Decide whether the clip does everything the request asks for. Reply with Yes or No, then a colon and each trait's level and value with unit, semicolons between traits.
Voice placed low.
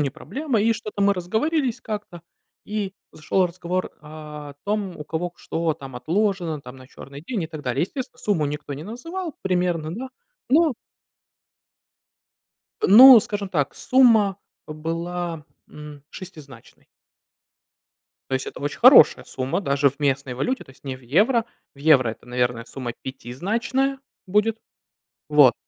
No: medium, 170 Hz